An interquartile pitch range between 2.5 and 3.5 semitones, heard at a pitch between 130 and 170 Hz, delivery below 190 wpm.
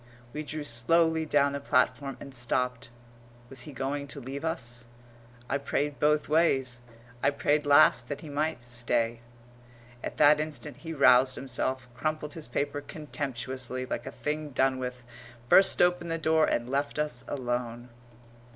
Yes: average, 3.2 semitones; medium, 140 Hz; average, 155 wpm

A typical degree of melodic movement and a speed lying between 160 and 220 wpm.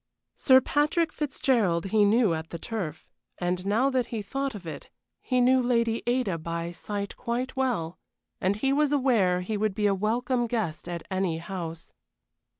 No: wide, 6.0 semitones; average, 170 wpm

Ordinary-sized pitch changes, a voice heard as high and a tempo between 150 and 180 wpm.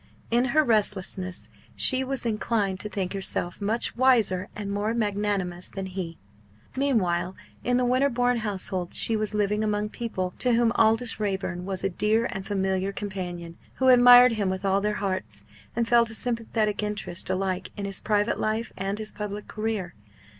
Yes: average, 3.3 semitones; high, 210 Hz; average, 170 wpm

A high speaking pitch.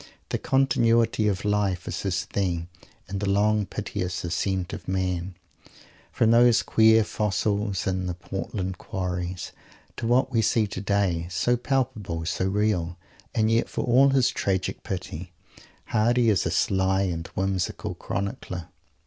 No: low, 100 Hz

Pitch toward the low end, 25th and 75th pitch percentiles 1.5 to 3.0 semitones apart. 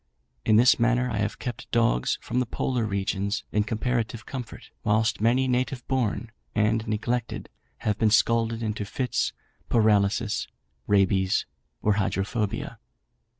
Yes: low, 110 Hz; narrow, 2.5 semitones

